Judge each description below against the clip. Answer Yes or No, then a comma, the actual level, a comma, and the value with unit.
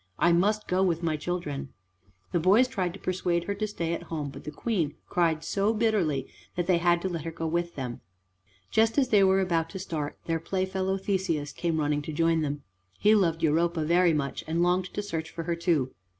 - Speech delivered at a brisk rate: Yes, fast, 215 wpm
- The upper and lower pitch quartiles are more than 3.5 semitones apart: No, average, 3.0 semitones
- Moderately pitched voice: Yes, medium, 170 Hz